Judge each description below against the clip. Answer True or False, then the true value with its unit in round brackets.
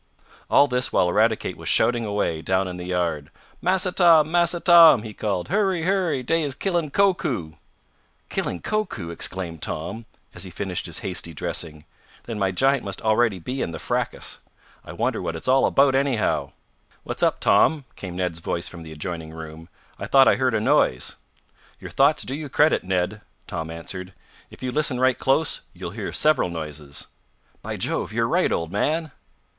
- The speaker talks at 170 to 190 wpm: True (180 wpm)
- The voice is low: True (110 Hz)